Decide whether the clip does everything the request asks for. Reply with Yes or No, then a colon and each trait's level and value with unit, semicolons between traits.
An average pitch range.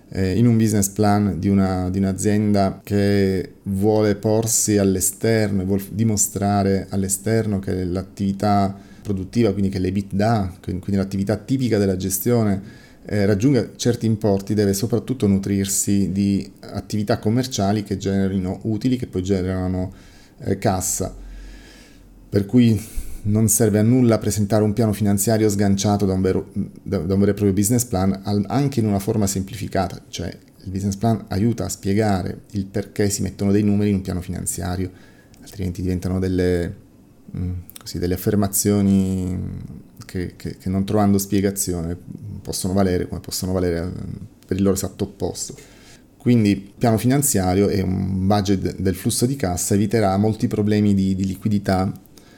No: narrow, 1.9 semitones